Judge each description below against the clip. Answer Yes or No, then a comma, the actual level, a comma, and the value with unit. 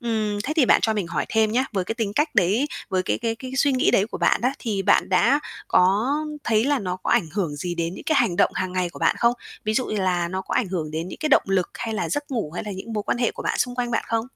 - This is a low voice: No, high, 215 Hz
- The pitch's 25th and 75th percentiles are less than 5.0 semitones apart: Yes, average, 4.6 semitones